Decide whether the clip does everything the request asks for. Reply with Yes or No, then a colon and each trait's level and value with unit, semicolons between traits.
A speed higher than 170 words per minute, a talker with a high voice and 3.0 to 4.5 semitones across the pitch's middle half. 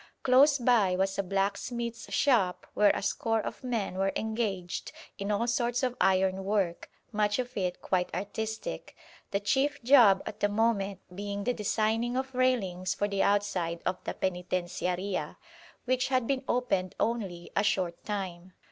No: average, 155 wpm; high, 205 Hz; average, 4.0 semitones